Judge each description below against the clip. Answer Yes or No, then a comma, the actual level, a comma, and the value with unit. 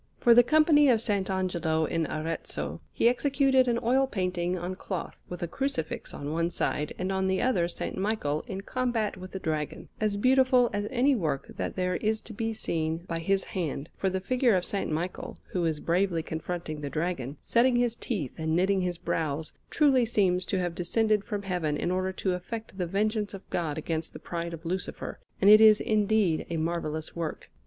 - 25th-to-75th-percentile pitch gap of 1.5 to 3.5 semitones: No, average, 4.8 semitones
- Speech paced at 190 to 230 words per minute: Yes, average, 200 wpm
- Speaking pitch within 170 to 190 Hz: Yes, medium, 185 Hz